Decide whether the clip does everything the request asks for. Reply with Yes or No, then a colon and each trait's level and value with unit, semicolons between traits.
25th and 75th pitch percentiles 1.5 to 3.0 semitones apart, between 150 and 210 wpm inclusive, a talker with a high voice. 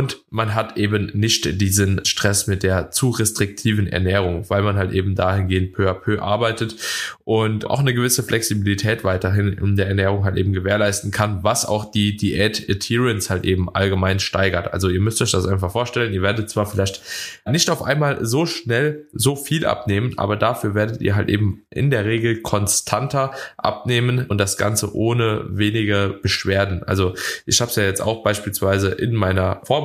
No: average, 2.7 semitones; average, 175 wpm; low, 105 Hz